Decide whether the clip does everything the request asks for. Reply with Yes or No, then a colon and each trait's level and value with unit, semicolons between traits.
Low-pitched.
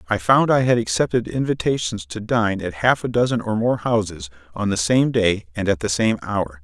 Yes: low, 105 Hz